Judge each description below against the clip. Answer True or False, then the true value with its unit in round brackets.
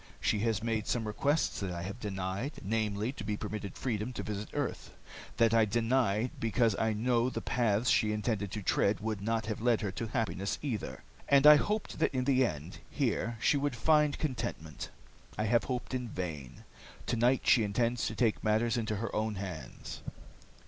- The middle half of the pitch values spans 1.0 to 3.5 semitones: True (2.9 semitones)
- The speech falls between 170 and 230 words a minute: True (185 wpm)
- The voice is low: True (110 Hz)